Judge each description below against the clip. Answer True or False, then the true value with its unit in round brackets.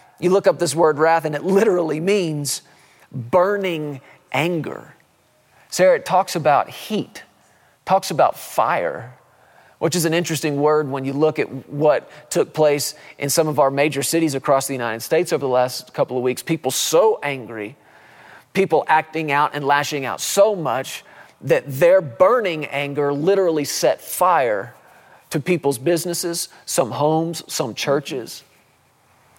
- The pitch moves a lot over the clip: False (3.5 semitones)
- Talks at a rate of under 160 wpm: True (150 wpm)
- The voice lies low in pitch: False (155 Hz)